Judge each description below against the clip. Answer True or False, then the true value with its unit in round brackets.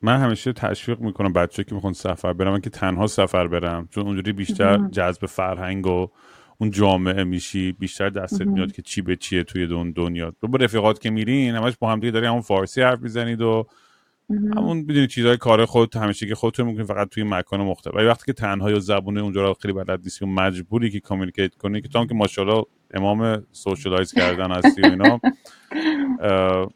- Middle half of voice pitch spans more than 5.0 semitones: False (3.4 semitones)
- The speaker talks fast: True (185 wpm)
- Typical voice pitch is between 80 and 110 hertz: True (100 Hz)